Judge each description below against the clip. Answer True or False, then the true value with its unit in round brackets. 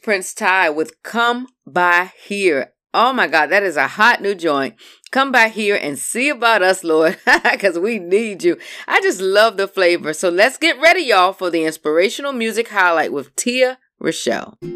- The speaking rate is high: False (185 wpm)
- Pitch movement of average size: False (6.0 semitones)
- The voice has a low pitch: False (205 Hz)